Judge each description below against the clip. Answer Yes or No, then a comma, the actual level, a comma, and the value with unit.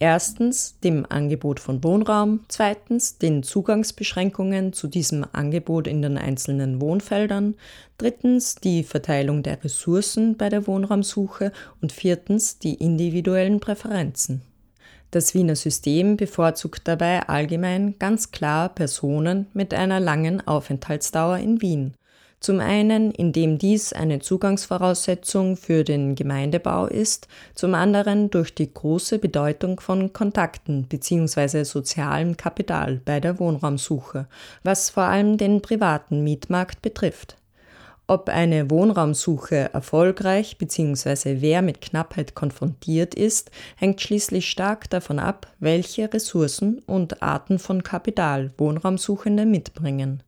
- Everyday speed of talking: No, slow, 115 wpm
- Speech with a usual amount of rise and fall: Yes, average, 4.8 semitones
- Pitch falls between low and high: Yes, medium, 175 Hz